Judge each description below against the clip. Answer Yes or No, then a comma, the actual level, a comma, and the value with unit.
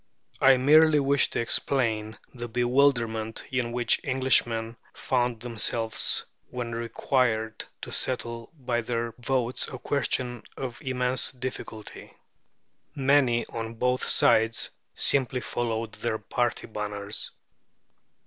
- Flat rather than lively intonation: Yes, narrow, 2.3 semitones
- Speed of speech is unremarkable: No, slow, 110 wpm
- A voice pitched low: Yes, low, 120 Hz